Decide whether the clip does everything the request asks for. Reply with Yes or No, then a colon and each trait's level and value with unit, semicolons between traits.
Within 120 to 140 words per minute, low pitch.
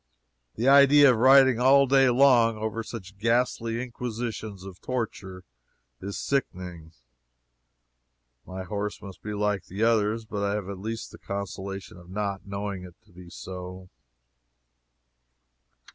Yes: slow, 135 wpm; low, 105 Hz